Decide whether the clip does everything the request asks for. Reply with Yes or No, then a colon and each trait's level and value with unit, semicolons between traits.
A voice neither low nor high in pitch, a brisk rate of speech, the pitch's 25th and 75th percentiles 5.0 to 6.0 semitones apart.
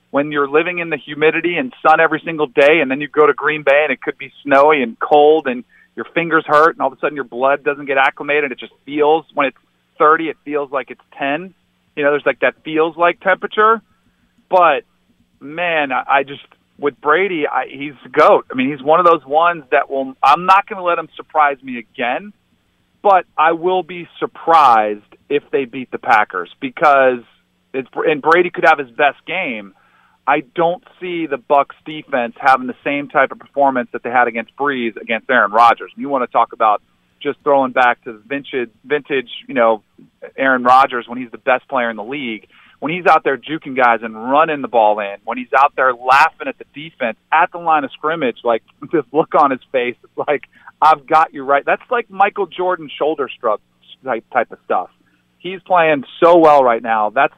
No: medium, 145 Hz; fast, 210 wpm; average, 4.3 semitones